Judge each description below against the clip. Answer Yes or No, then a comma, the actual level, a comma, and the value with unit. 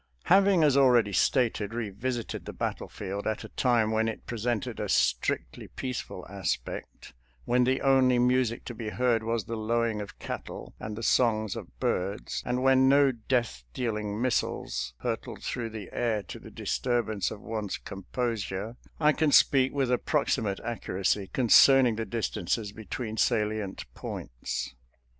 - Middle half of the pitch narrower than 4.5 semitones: Yes, average, 3.2 semitones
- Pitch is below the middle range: Yes, low, 115 Hz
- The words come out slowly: No, average, 160 wpm